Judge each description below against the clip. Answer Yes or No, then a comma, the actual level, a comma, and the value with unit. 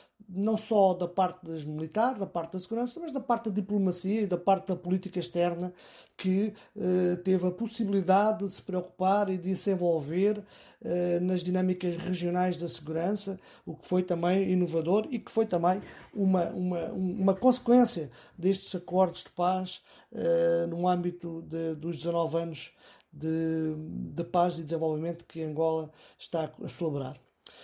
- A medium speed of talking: Yes, average, 155 wpm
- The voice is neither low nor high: Yes, medium, 180 Hz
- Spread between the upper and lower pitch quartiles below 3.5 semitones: Yes, narrow, 2.5 semitones